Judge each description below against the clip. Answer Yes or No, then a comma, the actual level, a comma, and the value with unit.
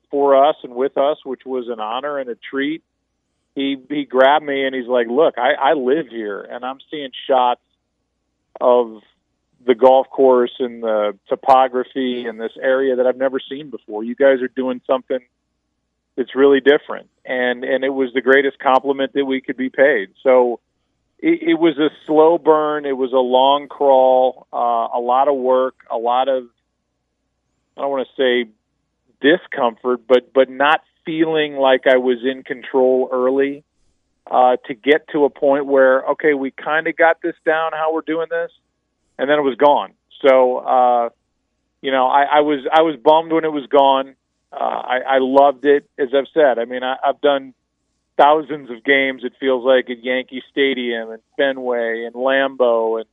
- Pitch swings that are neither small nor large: No, narrow, 2.1 semitones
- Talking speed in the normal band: Yes, average, 185 wpm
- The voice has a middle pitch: No, low, 130 Hz